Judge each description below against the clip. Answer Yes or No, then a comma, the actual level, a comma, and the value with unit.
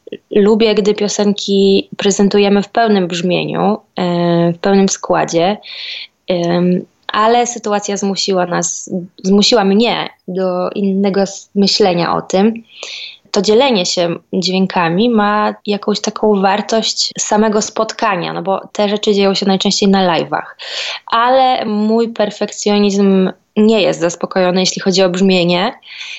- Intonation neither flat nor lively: No, narrow, 2.1 semitones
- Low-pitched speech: No, high, 200 Hz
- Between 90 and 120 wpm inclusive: Yes, average, 115 wpm